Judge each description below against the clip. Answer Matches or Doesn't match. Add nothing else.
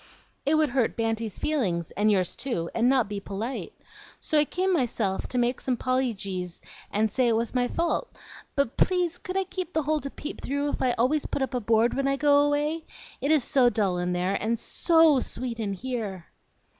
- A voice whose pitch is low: Doesn't match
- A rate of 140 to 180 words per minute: Doesn't match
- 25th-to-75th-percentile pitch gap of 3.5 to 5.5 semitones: Matches